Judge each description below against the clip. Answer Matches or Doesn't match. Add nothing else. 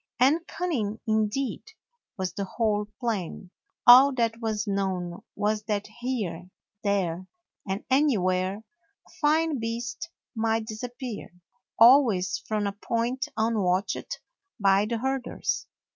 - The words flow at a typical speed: Doesn't match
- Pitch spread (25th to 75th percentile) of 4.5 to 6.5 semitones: Doesn't match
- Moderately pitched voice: Doesn't match